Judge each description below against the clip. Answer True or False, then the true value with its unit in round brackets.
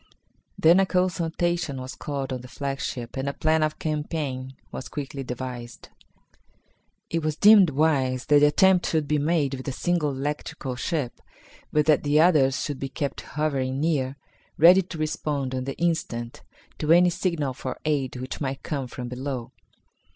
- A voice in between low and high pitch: True (145 Hz)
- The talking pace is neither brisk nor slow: True (165 wpm)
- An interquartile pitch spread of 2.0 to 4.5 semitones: True (3.4 semitones)